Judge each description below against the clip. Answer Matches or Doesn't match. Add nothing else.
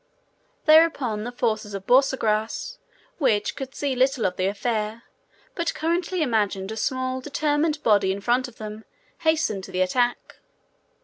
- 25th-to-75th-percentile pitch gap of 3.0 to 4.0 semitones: Doesn't match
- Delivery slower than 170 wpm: Matches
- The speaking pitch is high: Matches